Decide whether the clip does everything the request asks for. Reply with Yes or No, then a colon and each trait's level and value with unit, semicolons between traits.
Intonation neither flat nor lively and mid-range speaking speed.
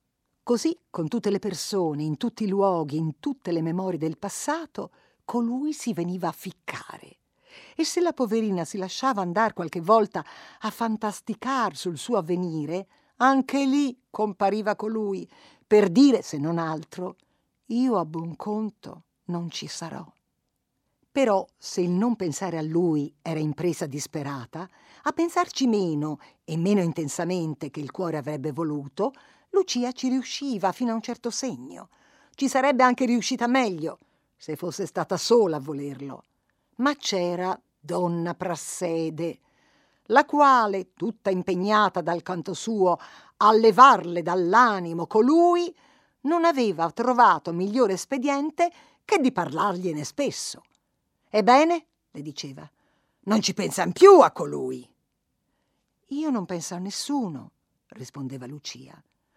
No: wide, 7.0 semitones; average, 130 wpm